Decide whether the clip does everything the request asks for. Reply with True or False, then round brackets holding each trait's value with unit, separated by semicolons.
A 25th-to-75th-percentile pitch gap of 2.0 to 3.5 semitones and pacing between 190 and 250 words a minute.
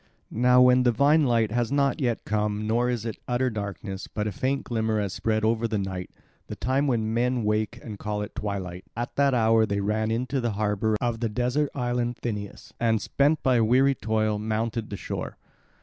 True (2.7 semitones; 195 wpm)